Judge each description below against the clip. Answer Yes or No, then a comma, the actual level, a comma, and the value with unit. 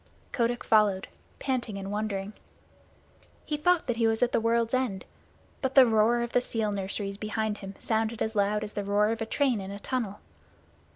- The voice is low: No, high, 220 Hz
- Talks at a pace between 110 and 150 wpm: No, average, 190 wpm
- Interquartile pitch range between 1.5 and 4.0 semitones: Yes, average, 2.7 semitones